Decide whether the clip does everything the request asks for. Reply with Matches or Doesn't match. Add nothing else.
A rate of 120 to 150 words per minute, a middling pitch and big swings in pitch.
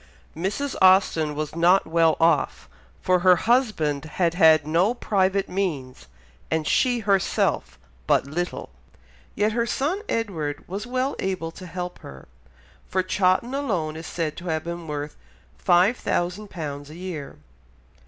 Doesn't match